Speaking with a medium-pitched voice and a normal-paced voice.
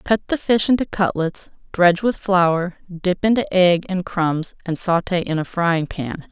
Yes: medium, 180 Hz; average, 180 wpm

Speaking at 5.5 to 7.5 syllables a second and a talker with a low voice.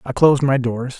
Yes: 5.7 syllables/s; low, 130 Hz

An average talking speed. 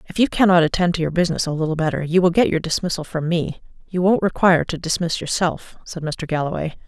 No: fast, 225 wpm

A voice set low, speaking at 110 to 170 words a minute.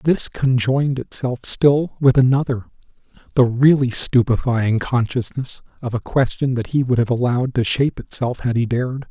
Yes: low, 125 Hz; average, 160 wpm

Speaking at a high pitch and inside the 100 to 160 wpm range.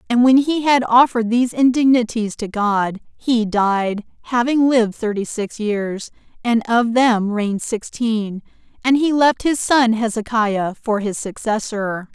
Yes: high, 230 Hz; average, 150 wpm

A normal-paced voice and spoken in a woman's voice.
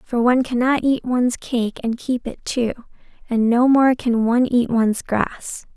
Yes: average, 190 wpm; female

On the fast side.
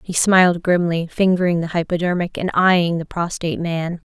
No: average, 160 wpm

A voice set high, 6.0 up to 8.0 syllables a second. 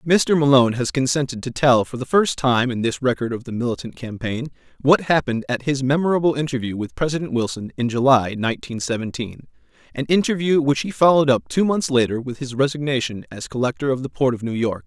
No: low, 135 Hz; 6.1 syllables/s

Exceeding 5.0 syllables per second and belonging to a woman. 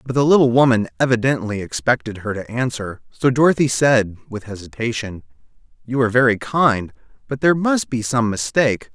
No: 5.6 syllables/s; male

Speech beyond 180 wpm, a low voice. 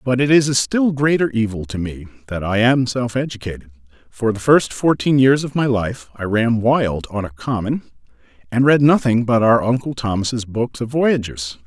Yes: average, 195 wpm; low, 120 Hz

